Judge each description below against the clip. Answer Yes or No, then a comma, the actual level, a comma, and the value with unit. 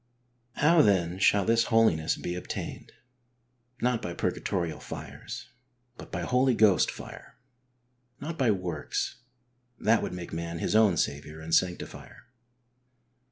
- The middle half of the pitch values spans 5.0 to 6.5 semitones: Yes, average, 5.3 semitones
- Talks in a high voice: No, very low, 95 Hz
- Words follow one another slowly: Yes, slow, 125 wpm